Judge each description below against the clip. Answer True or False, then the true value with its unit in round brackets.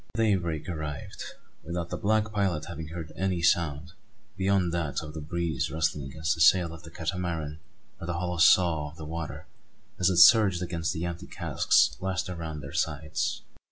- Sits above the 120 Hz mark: False (85 Hz)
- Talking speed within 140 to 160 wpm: False (175 wpm)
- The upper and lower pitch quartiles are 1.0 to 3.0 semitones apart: True (2.4 semitones)